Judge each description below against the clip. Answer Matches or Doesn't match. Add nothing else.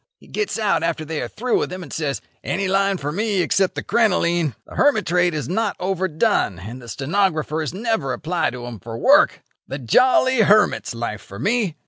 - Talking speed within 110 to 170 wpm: Doesn't match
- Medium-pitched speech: Matches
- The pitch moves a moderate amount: Doesn't match